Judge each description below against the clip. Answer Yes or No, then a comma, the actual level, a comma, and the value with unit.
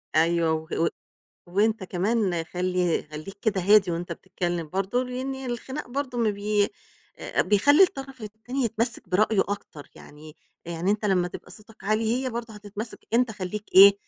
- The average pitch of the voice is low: No, high, 205 Hz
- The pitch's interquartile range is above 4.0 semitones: Yes, average, 4.4 semitones